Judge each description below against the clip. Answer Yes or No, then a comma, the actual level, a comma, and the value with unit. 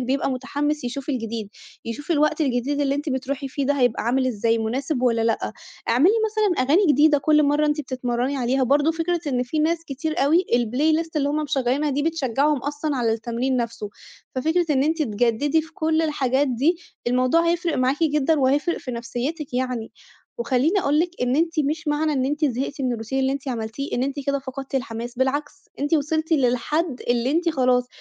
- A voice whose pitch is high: Yes, very high, 275 Hz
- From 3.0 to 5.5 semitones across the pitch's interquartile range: Yes, average, 3.4 semitones